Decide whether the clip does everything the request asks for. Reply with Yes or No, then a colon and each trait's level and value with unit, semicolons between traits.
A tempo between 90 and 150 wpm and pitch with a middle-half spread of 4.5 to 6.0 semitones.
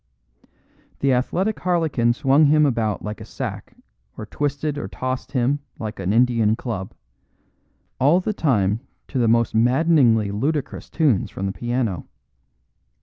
Yes: average, 140 wpm; average, 4.8 semitones